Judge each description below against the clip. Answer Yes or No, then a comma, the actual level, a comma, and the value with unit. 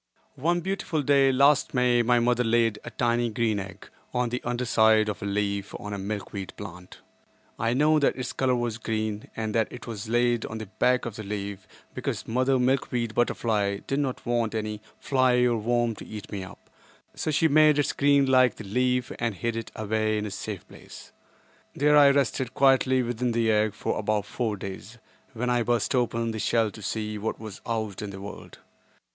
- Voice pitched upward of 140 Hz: No, low, 115 Hz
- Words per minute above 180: Yes, average, 200 wpm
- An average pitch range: Yes, average, 3.0 semitones